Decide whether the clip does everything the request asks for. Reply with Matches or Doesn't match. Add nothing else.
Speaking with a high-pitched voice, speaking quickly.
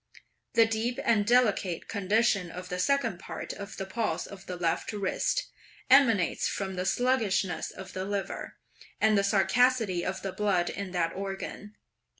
Doesn't match